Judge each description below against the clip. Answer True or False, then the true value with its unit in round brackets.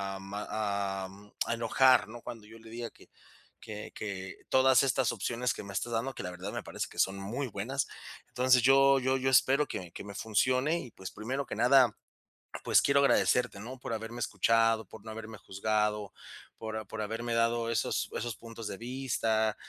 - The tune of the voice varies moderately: True (3.2 semitones)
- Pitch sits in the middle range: False (115 Hz)